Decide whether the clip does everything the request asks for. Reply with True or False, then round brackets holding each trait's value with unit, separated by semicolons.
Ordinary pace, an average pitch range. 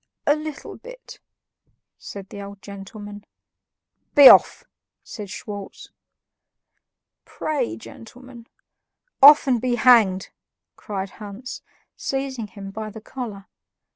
False (105 wpm; 4.6 semitones)